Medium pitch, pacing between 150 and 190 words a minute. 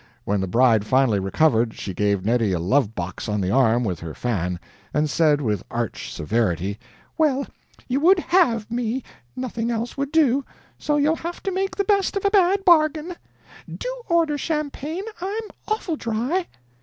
No: high, 230 Hz; average, 175 wpm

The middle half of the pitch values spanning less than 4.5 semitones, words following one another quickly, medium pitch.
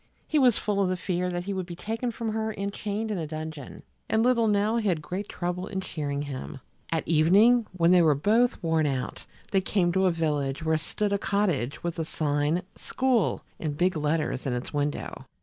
No: average, 4.9 semitones; fast, 210 wpm; medium, 180 Hz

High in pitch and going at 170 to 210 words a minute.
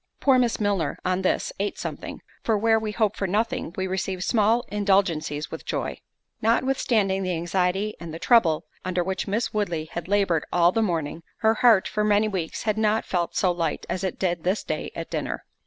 Yes: high, 195 Hz; average, 190 wpm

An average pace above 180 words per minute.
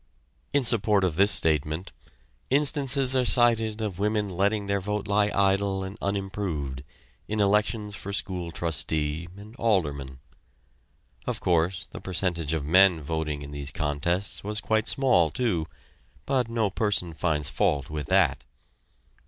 No: average, 140 wpm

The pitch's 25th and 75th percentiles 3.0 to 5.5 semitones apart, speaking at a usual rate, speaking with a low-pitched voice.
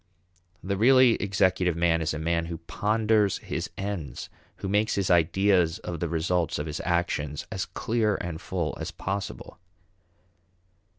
Yes: average, 3.5 semitones; average, 145 wpm; very low, 90 Hz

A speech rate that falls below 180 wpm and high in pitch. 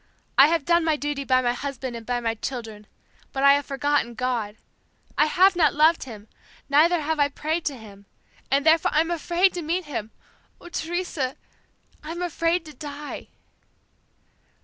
Yes: average, 170 wpm; very high, 290 Hz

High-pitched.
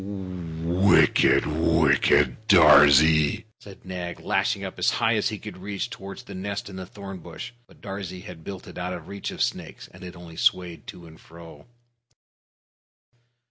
No: very low, 90 Hz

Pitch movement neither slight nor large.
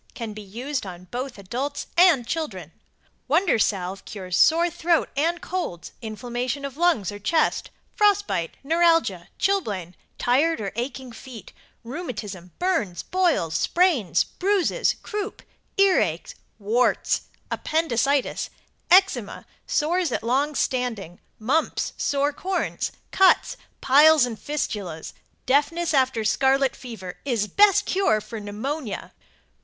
No: wide, 7.6 semitones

